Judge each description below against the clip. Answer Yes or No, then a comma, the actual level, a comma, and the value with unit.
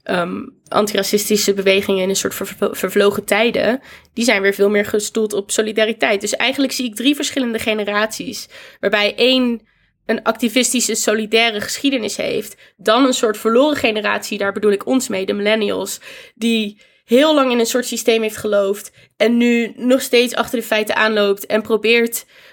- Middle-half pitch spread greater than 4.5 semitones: No, narrow, 2.6 semitones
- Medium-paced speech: Yes, average, 165 wpm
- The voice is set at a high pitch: Yes, high, 220 Hz